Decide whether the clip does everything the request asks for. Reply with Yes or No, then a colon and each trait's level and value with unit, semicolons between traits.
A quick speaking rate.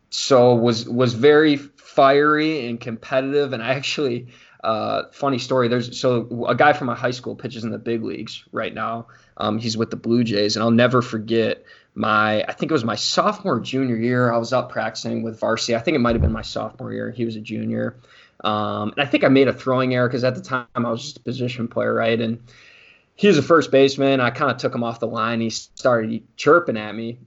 Yes: fast, 230 wpm